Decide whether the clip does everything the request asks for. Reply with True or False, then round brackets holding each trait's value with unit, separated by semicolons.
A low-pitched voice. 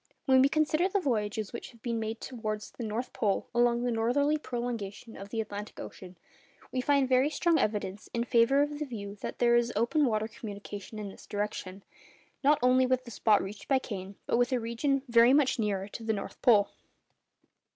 False (235 Hz)